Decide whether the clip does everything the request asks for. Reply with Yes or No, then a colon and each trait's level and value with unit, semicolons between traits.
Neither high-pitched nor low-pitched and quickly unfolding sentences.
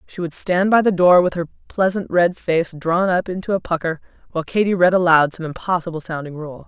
Yes: medium, 175 Hz; fast, 215 wpm